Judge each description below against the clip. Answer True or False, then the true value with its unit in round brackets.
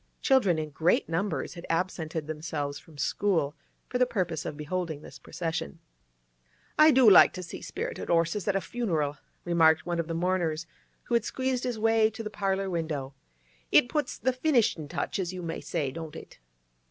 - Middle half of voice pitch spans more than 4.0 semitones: True (5.1 semitones)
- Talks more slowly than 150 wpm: False (180 wpm)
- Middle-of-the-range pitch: True (175 Hz)